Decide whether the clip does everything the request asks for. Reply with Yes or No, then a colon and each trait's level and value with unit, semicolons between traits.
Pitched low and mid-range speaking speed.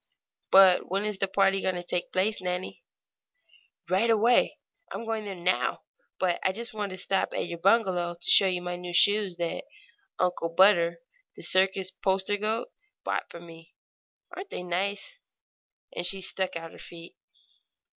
No: high, 190 Hz; average, 160 wpm